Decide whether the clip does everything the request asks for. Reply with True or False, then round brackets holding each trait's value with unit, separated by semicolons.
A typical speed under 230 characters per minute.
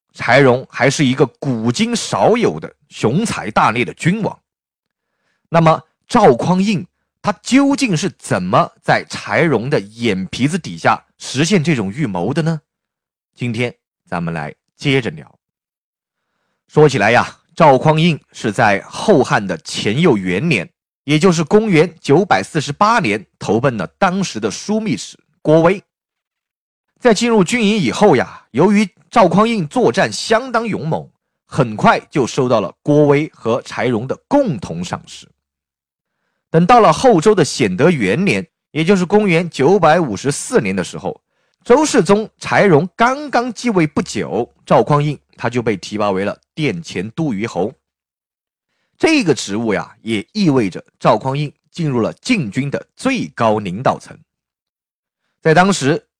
True (205 characters per minute)